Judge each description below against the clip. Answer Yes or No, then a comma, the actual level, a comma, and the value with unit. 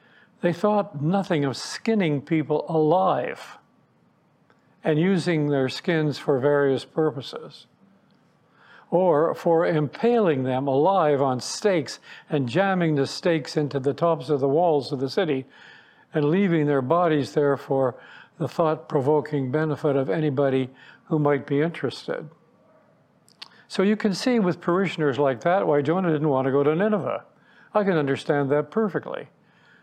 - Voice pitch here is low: No, medium, 155 Hz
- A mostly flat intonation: No, average, 3.6 semitones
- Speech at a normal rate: Yes, average, 145 wpm